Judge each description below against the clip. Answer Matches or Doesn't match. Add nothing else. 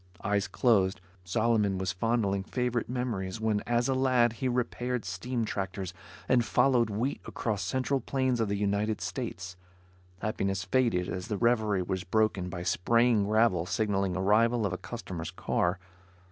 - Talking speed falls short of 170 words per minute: Matches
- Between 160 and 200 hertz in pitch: Doesn't match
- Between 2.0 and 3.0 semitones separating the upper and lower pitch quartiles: Doesn't match